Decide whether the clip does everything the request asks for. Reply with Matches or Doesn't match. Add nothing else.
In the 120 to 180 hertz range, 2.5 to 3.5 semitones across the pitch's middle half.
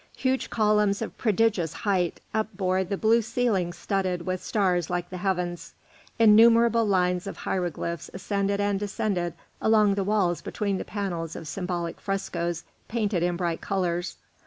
Doesn't match